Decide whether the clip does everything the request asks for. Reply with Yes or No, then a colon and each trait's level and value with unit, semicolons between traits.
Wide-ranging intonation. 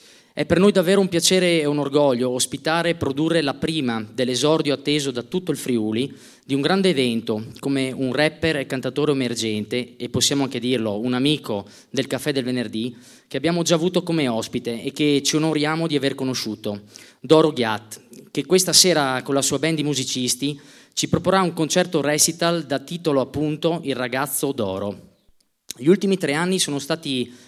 No: average, 4.1 semitones